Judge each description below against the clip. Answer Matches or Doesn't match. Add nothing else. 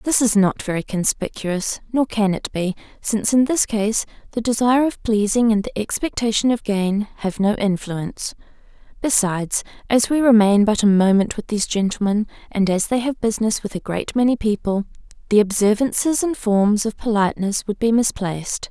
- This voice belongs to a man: Doesn't match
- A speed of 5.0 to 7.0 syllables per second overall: Matches